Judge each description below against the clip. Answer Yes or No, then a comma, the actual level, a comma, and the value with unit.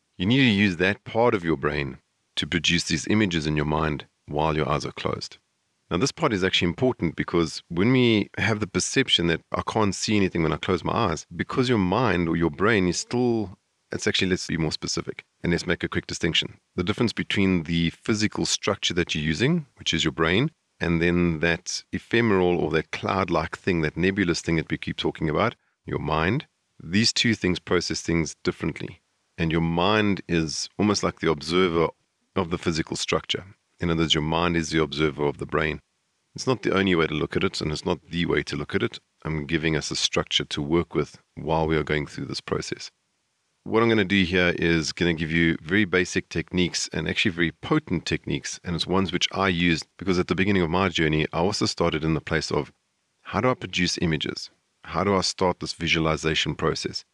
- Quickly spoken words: Yes, fast, 220 wpm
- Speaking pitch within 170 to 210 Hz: No, very low, 85 Hz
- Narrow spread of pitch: No, average, 3.5 semitones